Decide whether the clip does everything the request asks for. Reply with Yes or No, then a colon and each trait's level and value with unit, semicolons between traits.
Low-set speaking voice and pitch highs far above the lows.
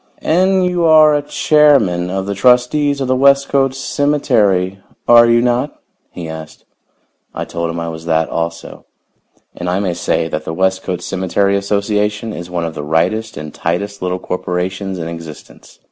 Yes: low, 100 Hz; wide, 6.8 semitones